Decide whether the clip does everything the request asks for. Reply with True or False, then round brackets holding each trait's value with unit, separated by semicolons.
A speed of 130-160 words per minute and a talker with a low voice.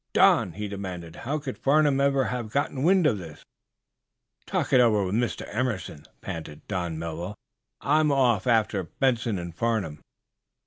True (150 wpm; 110 Hz)